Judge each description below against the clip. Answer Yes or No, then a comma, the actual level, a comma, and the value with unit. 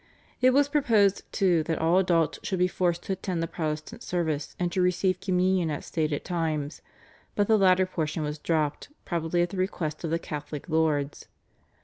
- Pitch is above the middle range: No, medium, 175 Hz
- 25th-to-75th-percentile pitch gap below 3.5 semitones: Yes, average, 3.0 semitones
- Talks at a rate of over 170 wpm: Yes, average, 185 wpm